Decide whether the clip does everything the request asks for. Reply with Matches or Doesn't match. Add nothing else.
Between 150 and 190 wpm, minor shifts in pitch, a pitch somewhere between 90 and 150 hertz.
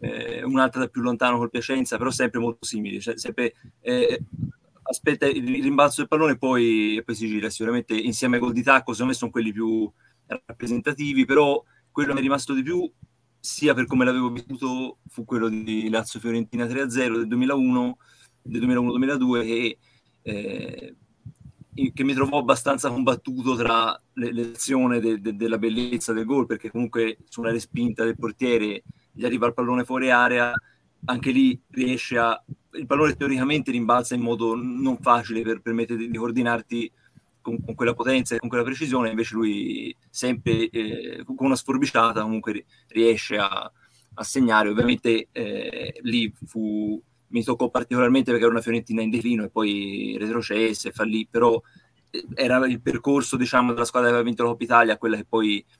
Matches